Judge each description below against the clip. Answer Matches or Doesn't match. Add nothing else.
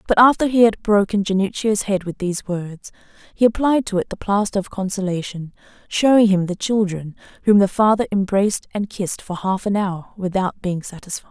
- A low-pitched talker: Doesn't match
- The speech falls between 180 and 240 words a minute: Matches